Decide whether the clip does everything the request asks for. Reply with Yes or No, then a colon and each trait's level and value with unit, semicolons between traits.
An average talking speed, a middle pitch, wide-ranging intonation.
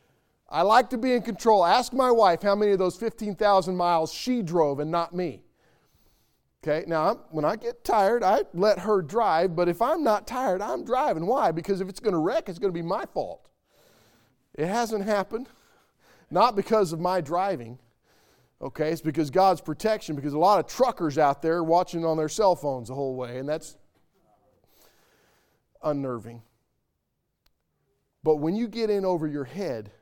Yes: average, 180 wpm; medium, 175 Hz; wide, 5.8 semitones